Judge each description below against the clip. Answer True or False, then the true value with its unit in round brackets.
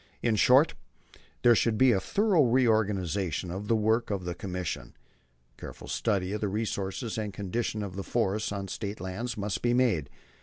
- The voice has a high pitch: False (105 Hz)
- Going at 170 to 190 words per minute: True (180 wpm)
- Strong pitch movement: False (3.4 semitones)